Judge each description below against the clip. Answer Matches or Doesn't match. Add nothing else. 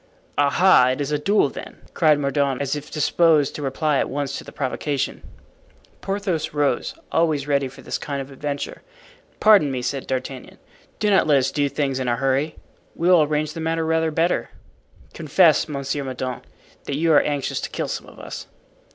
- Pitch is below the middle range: Doesn't match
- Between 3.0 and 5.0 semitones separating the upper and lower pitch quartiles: Doesn't match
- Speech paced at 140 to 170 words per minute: Doesn't match